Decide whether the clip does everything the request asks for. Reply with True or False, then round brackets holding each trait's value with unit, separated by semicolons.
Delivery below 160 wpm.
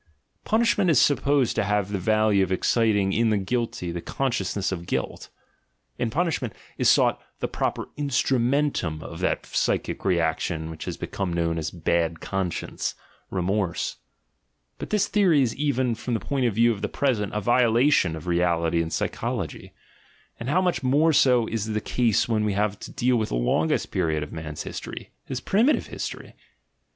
False (170 wpm)